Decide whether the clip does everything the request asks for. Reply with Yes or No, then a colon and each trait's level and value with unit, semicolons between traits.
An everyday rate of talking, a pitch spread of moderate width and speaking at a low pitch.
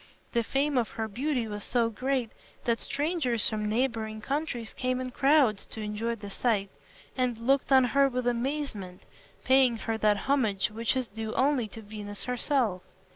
No: average, 170 wpm; average, 3.5 semitones; high, 235 Hz